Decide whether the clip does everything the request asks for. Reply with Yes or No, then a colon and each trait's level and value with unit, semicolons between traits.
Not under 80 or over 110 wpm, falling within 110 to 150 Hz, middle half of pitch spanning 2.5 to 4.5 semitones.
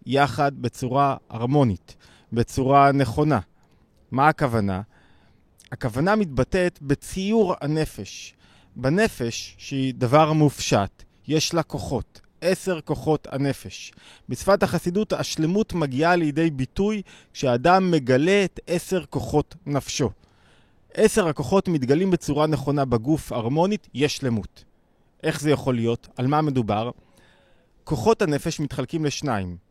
No: average, 105 wpm; medium, 140 Hz; average, 5.3 semitones